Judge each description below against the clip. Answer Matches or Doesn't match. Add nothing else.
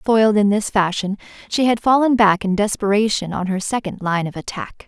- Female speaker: Matches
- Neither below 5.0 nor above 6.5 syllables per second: Matches